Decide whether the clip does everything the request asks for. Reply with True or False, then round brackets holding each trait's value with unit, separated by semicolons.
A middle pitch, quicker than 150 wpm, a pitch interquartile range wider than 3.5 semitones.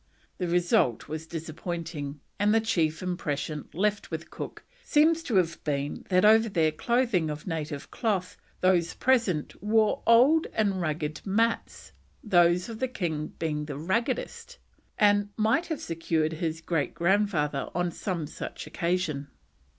False (175 Hz; 145 wpm; 5.2 semitones)